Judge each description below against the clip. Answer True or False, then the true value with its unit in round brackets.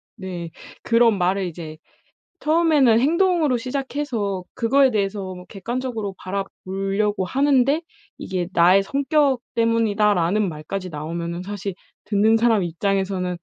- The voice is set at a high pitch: True (205 Hz)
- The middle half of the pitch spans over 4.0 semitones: True (5.2 semitones)